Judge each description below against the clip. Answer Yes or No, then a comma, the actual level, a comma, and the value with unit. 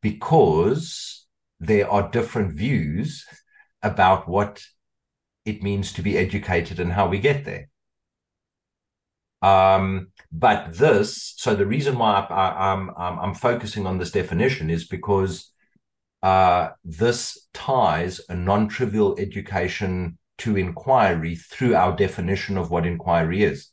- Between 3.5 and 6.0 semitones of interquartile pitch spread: No, average, 3.0 semitones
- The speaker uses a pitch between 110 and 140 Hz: No, very low, 95 Hz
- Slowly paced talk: Yes, slow, 125 wpm